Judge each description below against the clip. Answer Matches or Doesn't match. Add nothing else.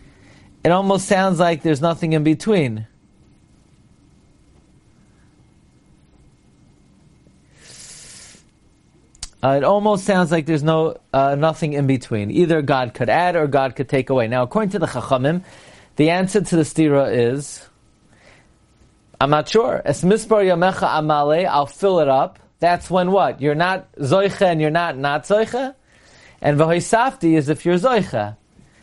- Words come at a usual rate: Matches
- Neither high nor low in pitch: Matches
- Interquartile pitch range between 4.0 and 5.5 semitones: Matches